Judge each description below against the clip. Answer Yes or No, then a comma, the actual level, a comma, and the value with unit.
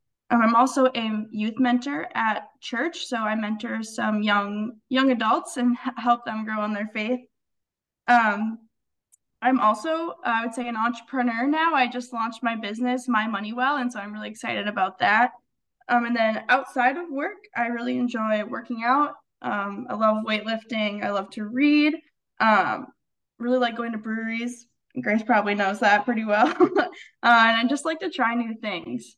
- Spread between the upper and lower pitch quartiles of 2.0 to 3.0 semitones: Yes, average, 2.7 semitones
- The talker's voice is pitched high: Yes, high, 235 Hz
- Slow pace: No, average, 175 wpm